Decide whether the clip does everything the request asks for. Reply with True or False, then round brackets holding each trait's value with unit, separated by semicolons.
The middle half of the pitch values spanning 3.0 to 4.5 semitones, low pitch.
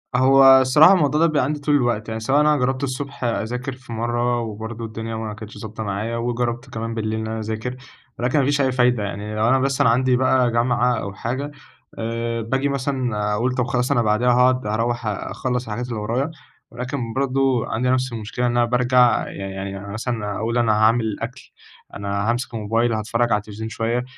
False (2.5 semitones; 120 Hz)